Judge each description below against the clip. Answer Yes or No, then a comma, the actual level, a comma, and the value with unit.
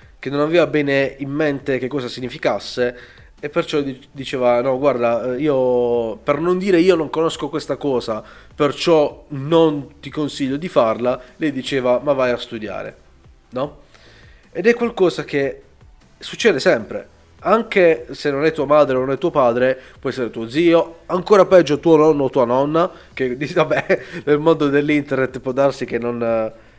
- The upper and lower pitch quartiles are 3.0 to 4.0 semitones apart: Yes, average, 3.6 semitones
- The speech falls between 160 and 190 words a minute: Yes, average, 165 wpm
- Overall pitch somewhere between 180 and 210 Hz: No, medium, 140 Hz